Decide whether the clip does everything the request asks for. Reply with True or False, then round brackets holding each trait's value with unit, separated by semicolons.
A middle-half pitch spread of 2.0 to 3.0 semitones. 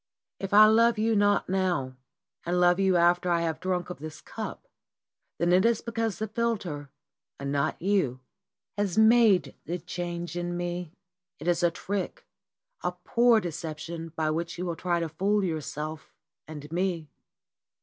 False (3.6 semitones)